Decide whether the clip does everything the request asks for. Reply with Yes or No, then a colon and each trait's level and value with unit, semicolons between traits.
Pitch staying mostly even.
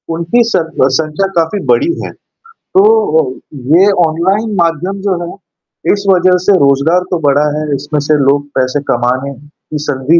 No: average, 4.7 semitones